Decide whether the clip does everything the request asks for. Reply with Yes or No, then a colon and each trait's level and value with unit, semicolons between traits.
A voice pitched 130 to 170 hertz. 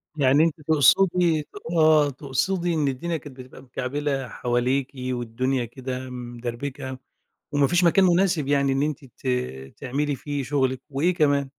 Yes: medium, 140 Hz